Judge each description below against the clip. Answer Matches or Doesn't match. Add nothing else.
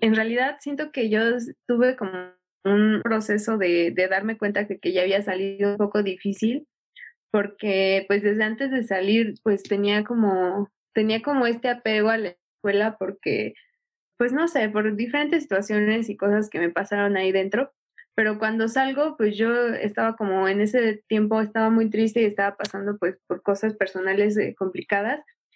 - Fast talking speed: Doesn't match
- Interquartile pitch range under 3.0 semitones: Matches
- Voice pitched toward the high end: Matches